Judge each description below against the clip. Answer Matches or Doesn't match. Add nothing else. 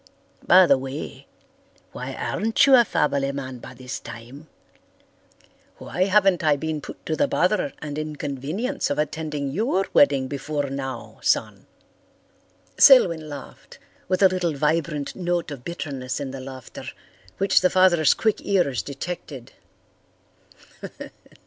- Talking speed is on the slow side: Matches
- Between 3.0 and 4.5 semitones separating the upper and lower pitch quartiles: Doesn't match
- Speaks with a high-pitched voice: Doesn't match